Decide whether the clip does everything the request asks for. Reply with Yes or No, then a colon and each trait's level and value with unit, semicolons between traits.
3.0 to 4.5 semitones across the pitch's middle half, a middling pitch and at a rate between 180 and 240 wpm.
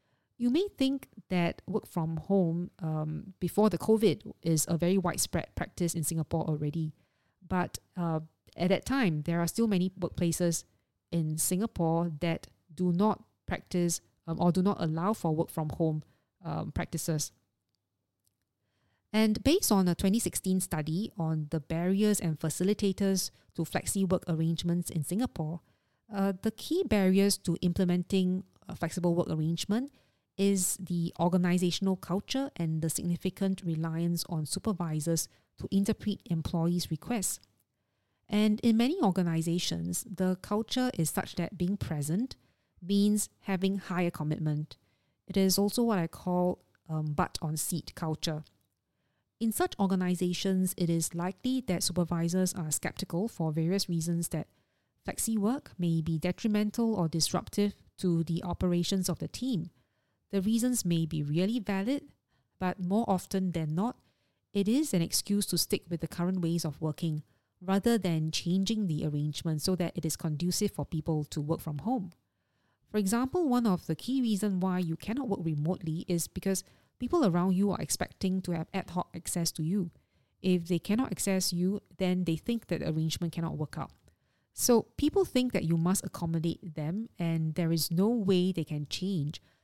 No: average, 3.3 semitones; medium, 175 Hz; average, 155 wpm